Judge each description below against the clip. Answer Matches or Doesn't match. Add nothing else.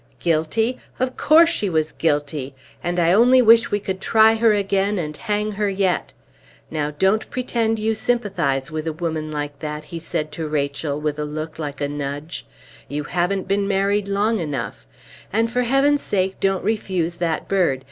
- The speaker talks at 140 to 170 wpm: Doesn't match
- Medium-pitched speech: Matches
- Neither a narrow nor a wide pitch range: Doesn't match